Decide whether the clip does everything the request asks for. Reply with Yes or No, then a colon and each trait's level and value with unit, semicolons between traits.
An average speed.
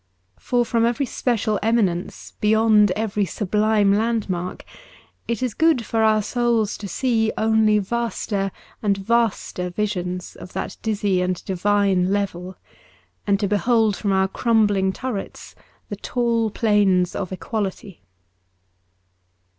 No: slow, 125 wpm